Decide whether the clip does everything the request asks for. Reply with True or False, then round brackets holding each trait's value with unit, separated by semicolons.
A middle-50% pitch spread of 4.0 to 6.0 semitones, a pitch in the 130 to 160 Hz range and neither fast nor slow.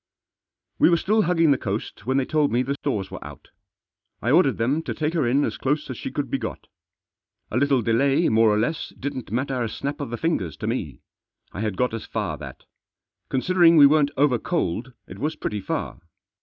False (4.9 semitones; 135 Hz; 210 wpm)